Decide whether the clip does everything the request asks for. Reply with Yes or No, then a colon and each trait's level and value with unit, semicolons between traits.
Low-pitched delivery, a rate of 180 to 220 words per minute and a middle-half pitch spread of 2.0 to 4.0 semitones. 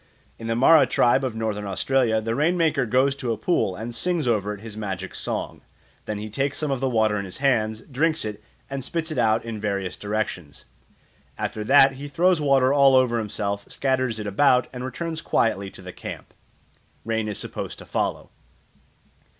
No: low, 115 Hz; average, 190 wpm; average, 4.4 semitones